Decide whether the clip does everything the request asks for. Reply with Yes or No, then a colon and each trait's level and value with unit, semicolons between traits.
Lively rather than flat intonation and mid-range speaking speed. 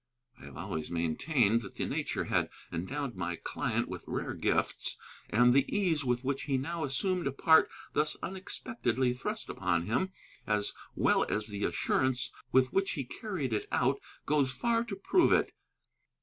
Yes: wide, 7.2 semitones; average, 165 wpm